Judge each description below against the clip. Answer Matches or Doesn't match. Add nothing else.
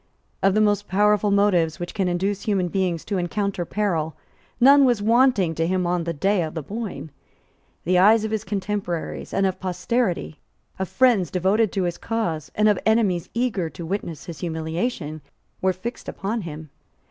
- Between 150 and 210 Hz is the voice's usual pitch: Matches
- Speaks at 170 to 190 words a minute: Matches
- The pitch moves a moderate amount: Matches